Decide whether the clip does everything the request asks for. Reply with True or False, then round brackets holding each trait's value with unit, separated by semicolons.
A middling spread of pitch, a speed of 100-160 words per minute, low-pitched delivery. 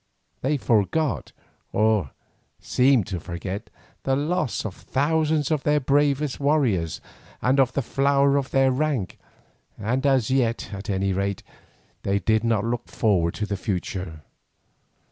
False (5.9 semitones; 140 wpm; 120 Hz)